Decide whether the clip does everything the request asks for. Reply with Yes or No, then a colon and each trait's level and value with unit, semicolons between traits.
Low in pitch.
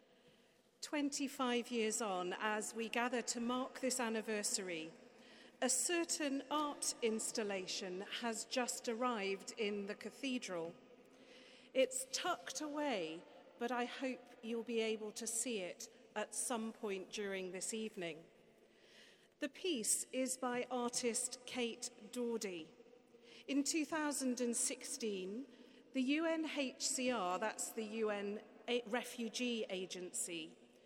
No: high, 240 Hz